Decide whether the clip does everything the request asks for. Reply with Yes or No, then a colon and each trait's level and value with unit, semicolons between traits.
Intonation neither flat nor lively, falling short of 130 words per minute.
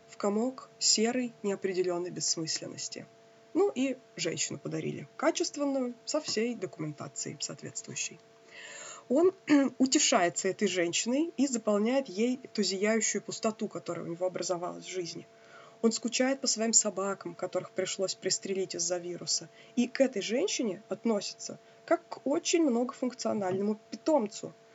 No: wide, 5.7 semitones; average, 120 wpm